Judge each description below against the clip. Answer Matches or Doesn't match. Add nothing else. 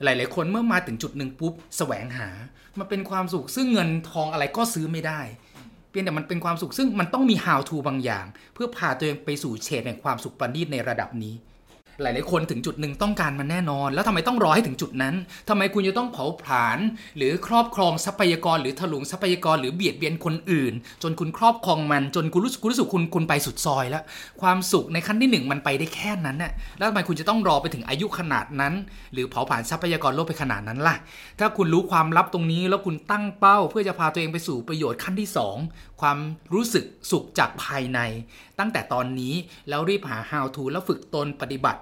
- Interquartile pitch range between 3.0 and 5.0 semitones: Doesn't match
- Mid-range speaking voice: Matches